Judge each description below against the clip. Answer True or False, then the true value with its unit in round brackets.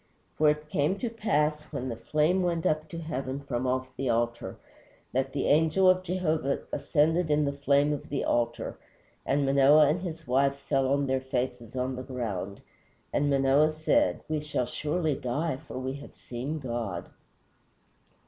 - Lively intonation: False (3.0 semitones)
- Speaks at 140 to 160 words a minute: False (170 wpm)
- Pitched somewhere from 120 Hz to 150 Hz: True (140 Hz)